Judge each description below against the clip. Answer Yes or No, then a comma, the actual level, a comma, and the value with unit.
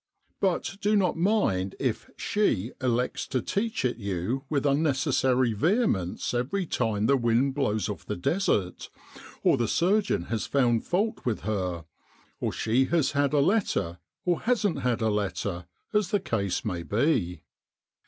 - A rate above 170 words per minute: No, average, 160 wpm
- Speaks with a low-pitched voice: Yes, low, 130 Hz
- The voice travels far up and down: Yes, wide, 8.8 semitones